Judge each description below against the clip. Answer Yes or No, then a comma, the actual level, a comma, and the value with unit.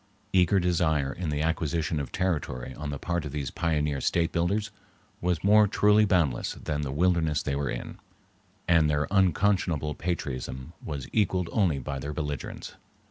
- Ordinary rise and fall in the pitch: Yes, average, 3.7 semitones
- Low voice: Yes, very low, 80 Hz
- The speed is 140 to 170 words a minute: Yes, average, 160 wpm